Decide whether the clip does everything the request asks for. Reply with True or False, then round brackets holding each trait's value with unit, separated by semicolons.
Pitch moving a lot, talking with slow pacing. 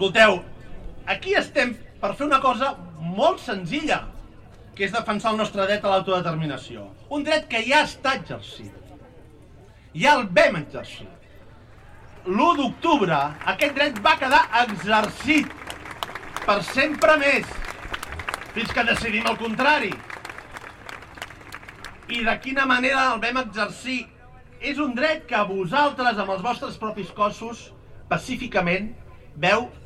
True (7.8 semitones; 125 wpm)